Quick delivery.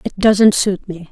Yes: fast, 215 wpm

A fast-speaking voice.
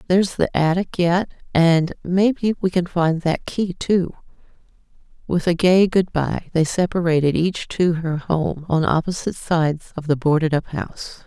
No: average, 165 wpm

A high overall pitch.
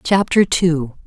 No: medium, 170 Hz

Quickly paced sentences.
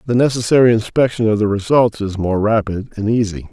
No: average, 190 wpm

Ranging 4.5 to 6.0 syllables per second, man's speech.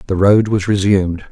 Yes: 5.5 syllables/s; male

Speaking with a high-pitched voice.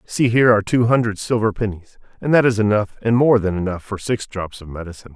No: low, 110 Hz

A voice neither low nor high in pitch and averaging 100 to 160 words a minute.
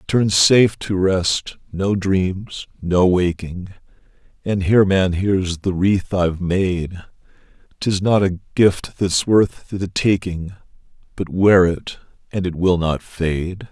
No: very low, 95 Hz; average, 140 wpm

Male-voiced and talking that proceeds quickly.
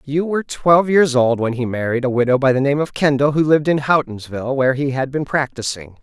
Yes: male; fast, 240 wpm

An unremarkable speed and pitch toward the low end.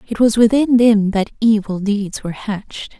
No: average, 180 wpm; high, 215 Hz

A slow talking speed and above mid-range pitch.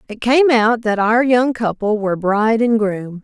No: fast, 205 wpm; high, 225 Hz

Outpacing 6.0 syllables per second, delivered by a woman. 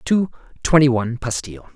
No: 6.6 syllables/s; male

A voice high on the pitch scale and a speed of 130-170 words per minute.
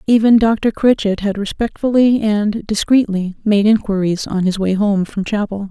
Yes: high, 210 Hz; average, 160 wpm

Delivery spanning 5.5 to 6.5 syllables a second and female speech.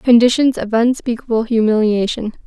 No: 5.2 syllables/s; female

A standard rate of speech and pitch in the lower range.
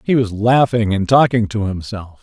Yes: average, 190 wpm; low, 110 Hz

